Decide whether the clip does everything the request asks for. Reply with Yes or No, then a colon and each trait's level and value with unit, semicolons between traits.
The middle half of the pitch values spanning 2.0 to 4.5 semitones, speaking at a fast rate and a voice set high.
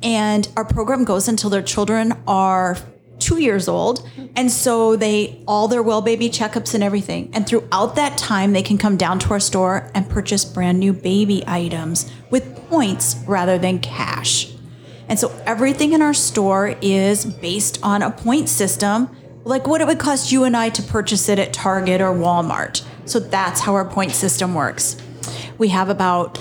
No: average, 3.7 semitones; average, 180 wpm; high, 200 Hz